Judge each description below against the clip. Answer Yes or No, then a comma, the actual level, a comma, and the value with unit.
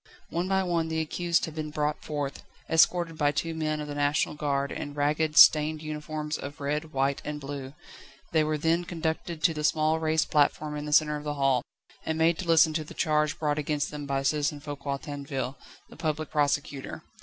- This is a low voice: No, medium, 150 Hz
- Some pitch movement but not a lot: No, narrow, 1.6 semitones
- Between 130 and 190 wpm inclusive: No, average, 200 wpm